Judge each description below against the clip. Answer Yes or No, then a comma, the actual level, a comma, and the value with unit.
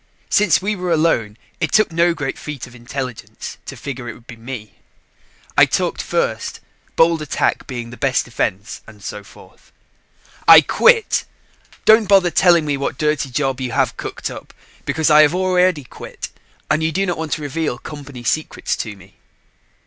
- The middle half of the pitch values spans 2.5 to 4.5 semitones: No, wide, 5.6 semitones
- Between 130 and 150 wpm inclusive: No, average, 175 wpm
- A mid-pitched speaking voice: Yes, medium, 145 Hz